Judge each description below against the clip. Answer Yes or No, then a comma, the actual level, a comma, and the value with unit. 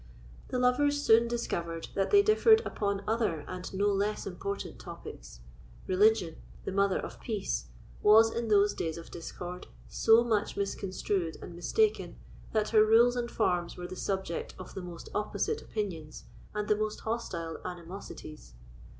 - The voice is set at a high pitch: Yes, high, 200 Hz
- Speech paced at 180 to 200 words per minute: No, average, 150 wpm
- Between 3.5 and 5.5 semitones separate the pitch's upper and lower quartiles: Yes, average, 4.0 semitones